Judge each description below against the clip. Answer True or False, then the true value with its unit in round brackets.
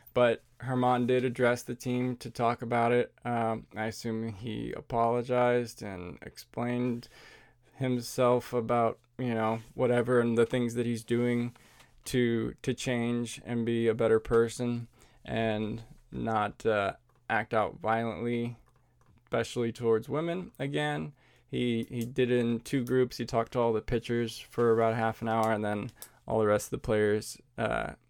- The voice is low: True (120 Hz)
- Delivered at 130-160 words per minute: True (155 wpm)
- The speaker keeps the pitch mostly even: True (1.4 semitones)